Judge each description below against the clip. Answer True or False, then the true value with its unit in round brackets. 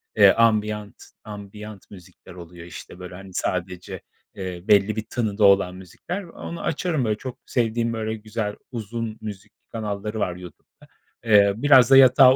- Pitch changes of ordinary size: True (3.2 semitones)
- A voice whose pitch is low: True (105 Hz)